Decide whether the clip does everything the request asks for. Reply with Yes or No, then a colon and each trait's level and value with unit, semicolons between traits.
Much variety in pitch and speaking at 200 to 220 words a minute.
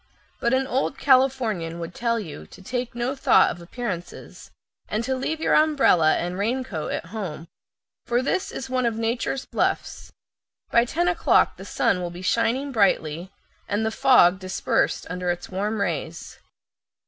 No: wide, 6.3 semitones; average, 160 wpm